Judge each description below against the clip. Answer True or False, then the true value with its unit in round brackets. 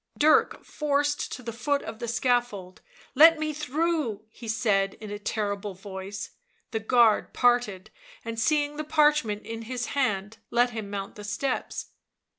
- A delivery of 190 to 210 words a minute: False (160 wpm)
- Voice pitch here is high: True (230 Hz)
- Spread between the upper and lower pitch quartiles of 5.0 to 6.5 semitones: True (5.5 semitones)